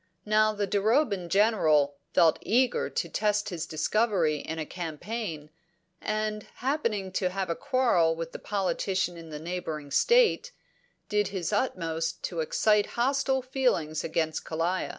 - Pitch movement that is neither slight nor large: Yes, average, 5.0 semitones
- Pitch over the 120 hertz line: Yes, high, 190 Hz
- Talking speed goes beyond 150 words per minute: No, average, 140 wpm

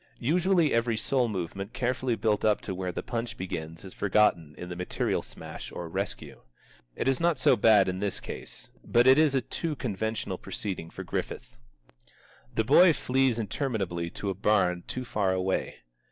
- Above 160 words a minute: Yes, average, 175 wpm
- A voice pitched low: Yes, low, 105 Hz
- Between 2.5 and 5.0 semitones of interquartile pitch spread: No, wide, 5.5 semitones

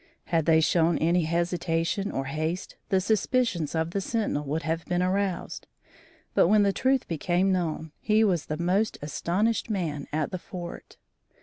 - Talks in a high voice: No, medium, 175 Hz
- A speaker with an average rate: Yes, average, 165 wpm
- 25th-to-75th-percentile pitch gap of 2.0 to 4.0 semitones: Yes, average, 3.5 semitones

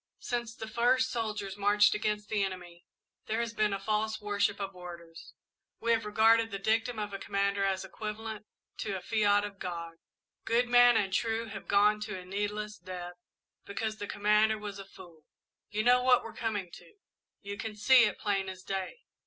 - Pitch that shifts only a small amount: Yes, narrow, 2.2 semitones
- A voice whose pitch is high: Yes, high, 210 Hz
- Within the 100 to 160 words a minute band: No, average, 185 wpm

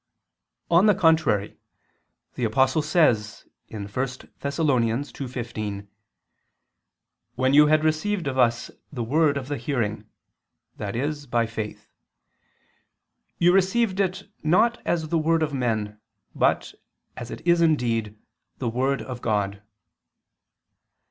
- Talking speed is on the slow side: Yes, slow, 115 wpm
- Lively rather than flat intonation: Yes, wide, 5.8 semitones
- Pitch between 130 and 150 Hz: Yes, low, 135 Hz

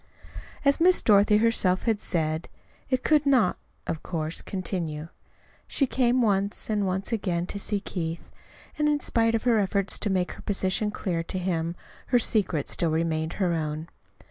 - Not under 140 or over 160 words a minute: No, average, 170 wpm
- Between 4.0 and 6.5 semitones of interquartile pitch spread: Yes, average, 5.1 semitones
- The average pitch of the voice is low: No, high, 195 Hz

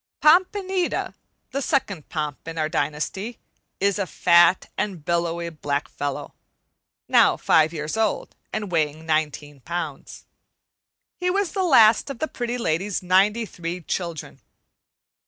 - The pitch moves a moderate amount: No, wide, 6.5 semitones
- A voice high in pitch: No, medium, 175 Hz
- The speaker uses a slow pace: Yes, slow, 130 wpm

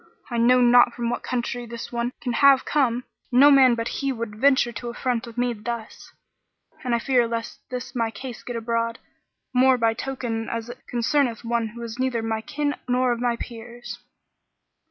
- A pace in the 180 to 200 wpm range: Yes, average, 190 wpm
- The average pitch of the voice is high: Yes, high, 240 Hz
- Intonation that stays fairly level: Yes, narrow, 1.5 semitones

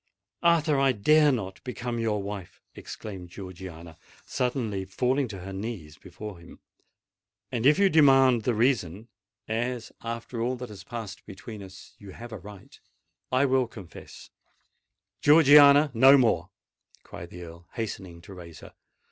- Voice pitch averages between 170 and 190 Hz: No, low, 110 Hz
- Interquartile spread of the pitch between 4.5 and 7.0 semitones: Yes, average, 5.1 semitones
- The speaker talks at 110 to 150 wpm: Yes, average, 140 wpm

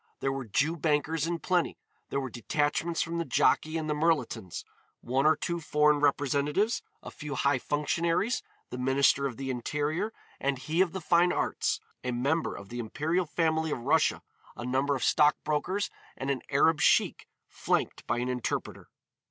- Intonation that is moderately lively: Yes, average, 3.5 semitones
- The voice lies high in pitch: No, medium, 150 Hz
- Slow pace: No, average, 175 wpm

